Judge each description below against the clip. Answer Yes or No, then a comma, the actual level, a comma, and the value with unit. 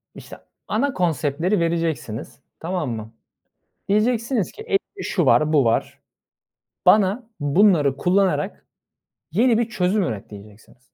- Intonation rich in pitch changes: Yes, wide, 7.2 semitones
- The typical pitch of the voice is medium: Yes, medium, 180 Hz